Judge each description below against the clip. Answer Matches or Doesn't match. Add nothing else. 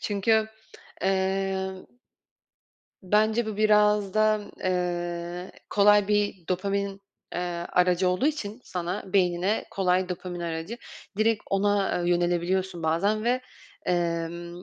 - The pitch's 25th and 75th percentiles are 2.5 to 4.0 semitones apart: Matches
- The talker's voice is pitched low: Doesn't match